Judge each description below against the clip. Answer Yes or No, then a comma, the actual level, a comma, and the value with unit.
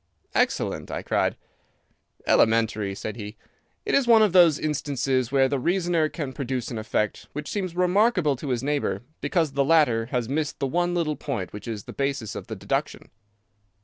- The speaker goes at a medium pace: Yes, average, 180 wpm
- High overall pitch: No, medium, 140 Hz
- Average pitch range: No, wide, 5.8 semitones